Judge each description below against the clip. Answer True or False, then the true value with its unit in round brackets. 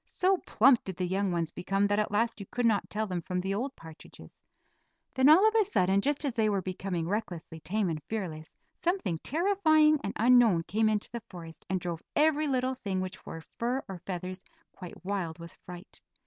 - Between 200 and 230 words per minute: True (205 wpm)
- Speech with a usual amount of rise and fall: False (5.7 semitones)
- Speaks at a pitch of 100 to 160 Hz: False (200 Hz)